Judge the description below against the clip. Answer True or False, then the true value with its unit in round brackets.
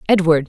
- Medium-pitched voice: True (170 Hz)